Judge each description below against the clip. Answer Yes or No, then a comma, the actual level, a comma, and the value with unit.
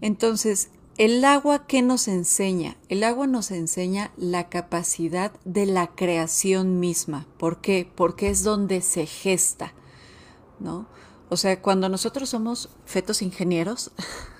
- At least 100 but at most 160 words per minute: Yes, average, 130 wpm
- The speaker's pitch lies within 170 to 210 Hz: Yes, high, 190 Hz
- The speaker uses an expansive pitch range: No, average, 3.6 semitones